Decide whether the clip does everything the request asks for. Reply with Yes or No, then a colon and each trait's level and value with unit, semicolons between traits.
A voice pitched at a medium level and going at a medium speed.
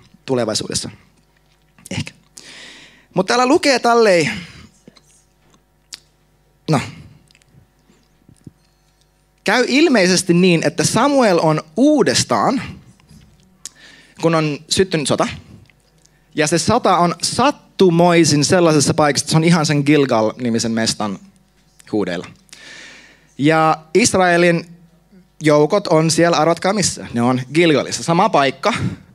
No: medium, 165 Hz; slow, 90 wpm